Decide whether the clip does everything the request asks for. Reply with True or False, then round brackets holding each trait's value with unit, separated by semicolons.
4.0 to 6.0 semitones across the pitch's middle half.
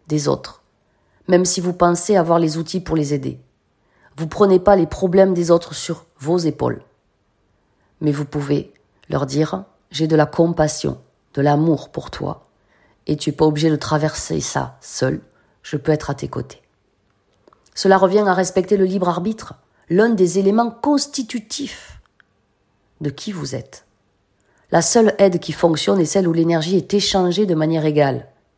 True (4.4 semitones)